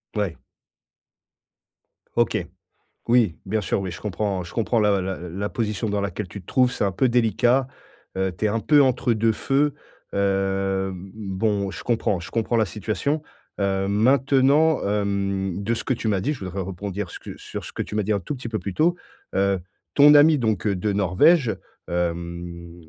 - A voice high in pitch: No, low, 105 Hz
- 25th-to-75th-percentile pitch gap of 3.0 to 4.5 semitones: Yes, average, 3.5 semitones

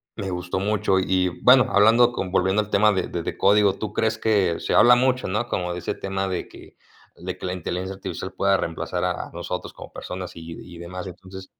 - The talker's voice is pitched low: Yes, very low, 95 Hz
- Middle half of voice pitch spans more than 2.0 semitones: Yes, narrow, 2.6 semitones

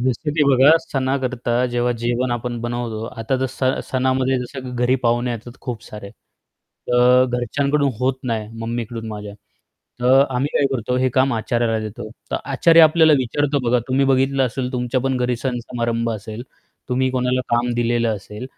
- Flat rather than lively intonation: Yes, narrow, 1.9 semitones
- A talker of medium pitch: No, low, 125 Hz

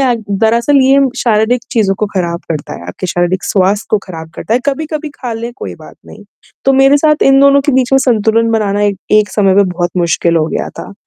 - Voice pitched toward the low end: No, high, 220 Hz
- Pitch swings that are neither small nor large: No, wide, 5.9 semitones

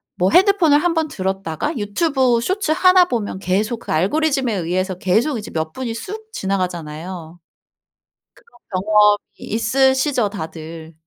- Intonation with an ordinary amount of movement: No, wide, 7.7 semitones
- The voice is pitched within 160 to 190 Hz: No, high, 215 Hz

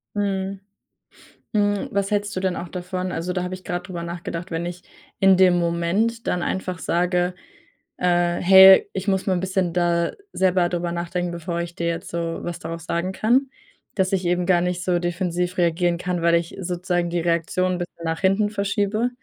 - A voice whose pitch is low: No, medium, 180 Hz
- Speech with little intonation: Yes, narrow, 1.7 semitones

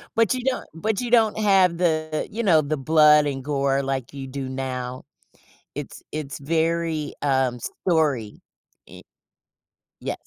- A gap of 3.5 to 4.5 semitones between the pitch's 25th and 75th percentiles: Yes, average, 4.0 semitones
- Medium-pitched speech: Yes, medium, 150 Hz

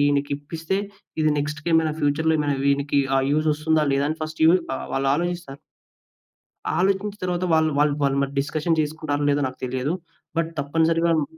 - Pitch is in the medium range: Yes, medium, 150 Hz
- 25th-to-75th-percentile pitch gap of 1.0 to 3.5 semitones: Yes, narrow, 2.4 semitones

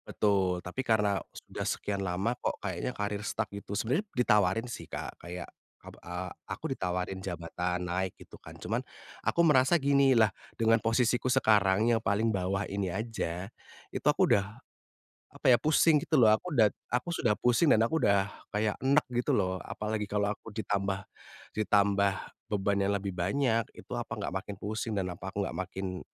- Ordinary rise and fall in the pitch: Yes, average, 3.2 semitones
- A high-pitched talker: No, low, 105 Hz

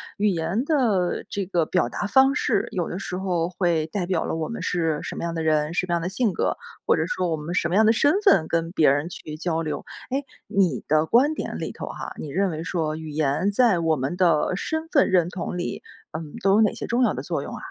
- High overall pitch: No, medium, 175 Hz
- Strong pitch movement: No, average, 3.8 semitones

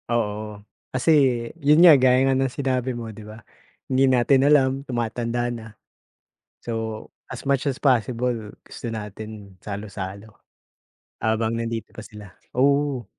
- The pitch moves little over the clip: No, average, 3.2 semitones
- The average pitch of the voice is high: No, low, 120 Hz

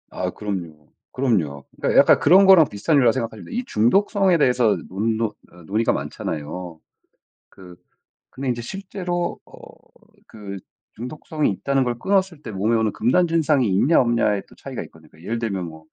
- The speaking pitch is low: Yes, low, 115 Hz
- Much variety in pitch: Yes, wide, 7.8 semitones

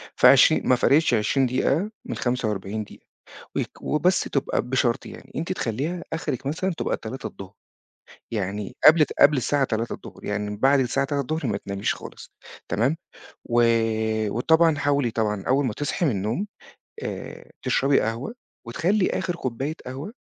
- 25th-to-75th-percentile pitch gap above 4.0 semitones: Yes, average, 5.3 semitones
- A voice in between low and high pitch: No, low, 130 Hz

